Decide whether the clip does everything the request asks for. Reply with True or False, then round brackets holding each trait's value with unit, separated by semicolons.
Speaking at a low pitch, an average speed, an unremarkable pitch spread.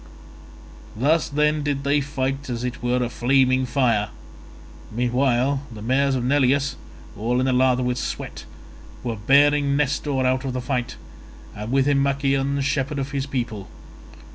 False (130 Hz; 155 wpm; 2.1 semitones)